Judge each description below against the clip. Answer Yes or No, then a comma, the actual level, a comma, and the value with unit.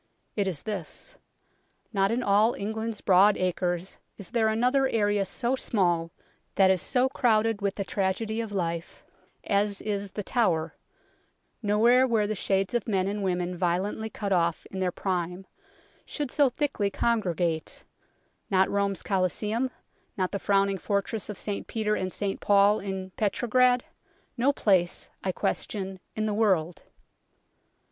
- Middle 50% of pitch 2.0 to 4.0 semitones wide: Yes, average, 2.8 semitones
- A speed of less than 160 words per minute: Yes, average, 150 wpm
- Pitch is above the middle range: Yes, high, 200 Hz